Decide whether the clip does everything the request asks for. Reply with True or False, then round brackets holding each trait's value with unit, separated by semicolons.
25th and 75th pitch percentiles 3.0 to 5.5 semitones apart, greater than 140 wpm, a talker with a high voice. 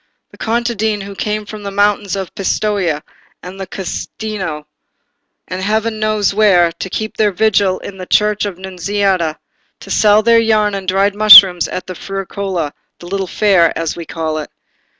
False (2.5 semitones; 170 wpm; 195 Hz)